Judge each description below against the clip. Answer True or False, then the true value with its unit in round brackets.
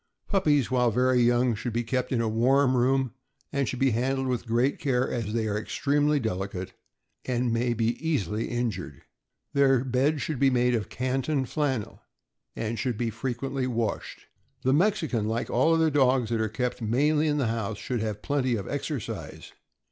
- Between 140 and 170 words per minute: False (180 wpm)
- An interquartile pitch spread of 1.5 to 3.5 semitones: True (2.9 semitones)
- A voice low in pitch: True (125 Hz)